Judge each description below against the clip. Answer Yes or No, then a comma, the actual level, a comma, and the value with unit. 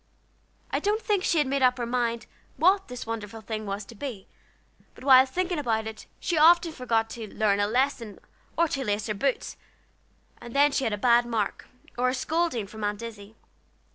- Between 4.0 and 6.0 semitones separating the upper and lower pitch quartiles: Yes, average, 4.5 semitones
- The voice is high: Yes, high, 240 Hz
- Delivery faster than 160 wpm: Yes, average, 200 wpm